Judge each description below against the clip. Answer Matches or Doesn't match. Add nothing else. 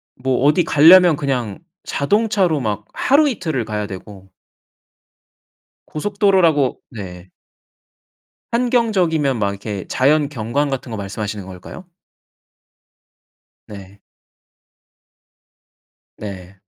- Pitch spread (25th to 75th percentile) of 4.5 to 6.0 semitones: Doesn't match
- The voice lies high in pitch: Doesn't match